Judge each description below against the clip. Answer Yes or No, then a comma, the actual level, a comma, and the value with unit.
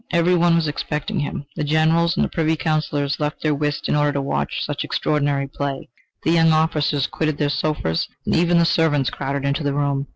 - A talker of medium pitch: Yes, medium, 150 Hz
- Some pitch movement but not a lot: No, narrow, 2.3 semitones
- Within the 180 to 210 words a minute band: Yes, average, 200 wpm